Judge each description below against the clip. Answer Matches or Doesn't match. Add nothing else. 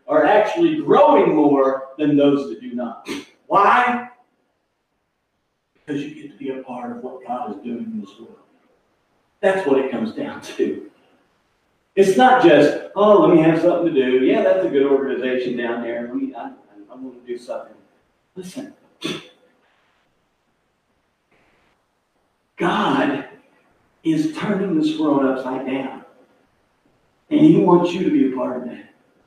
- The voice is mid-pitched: Matches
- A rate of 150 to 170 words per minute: Matches